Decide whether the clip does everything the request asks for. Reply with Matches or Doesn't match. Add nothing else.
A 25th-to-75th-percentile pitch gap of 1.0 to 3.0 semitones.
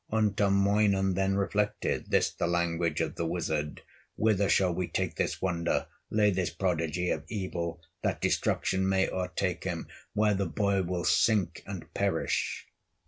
Matches